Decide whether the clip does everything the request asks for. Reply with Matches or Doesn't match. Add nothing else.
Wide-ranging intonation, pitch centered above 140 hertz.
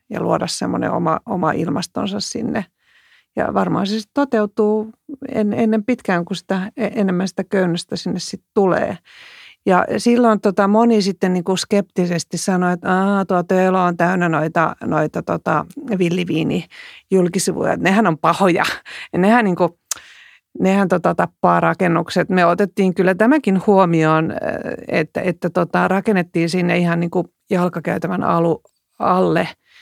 Doesn't match